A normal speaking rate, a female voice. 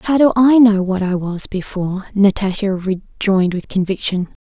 Yes: average, 160 wpm; female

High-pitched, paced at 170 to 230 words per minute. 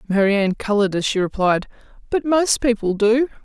No: high, 220 Hz; average, 155 wpm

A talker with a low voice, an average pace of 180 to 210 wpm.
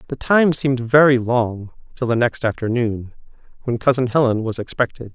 No: low, 120 Hz; average, 165 wpm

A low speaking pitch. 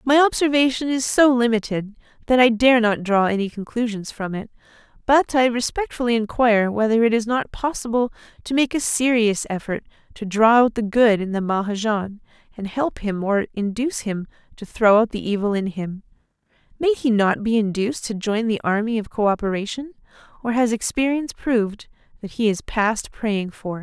No: high, 225 Hz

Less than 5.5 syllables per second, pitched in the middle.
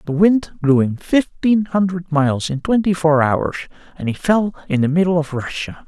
Yes: 4.9 syllables/s; medium, 165 Hz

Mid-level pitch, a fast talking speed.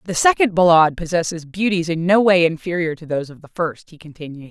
Yes: medium, 170 Hz; fast, 215 wpm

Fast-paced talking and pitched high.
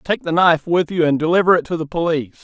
No: fast, 270 wpm; medium, 165 Hz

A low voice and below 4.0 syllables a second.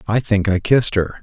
No: low, 105 Hz; 5.9 syllables/s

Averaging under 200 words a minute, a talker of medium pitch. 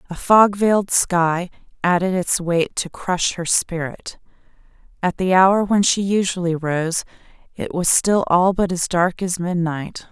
Yes: average, 160 wpm; medium, 180 Hz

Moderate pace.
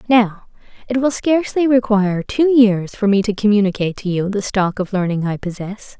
Yes: average, 190 wpm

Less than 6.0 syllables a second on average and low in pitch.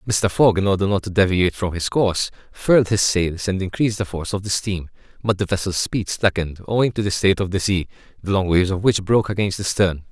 No: 6.4 syllables/s; very low, 95 Hz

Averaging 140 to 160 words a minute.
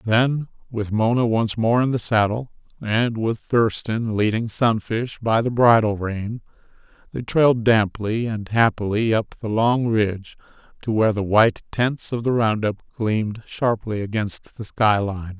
Yes: average, 155 wpm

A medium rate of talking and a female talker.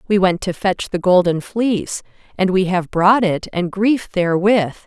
Yes: average, 185 wpm; female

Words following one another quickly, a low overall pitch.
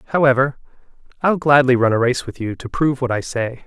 Yes: fast, 215 wpm; low, 130 Hz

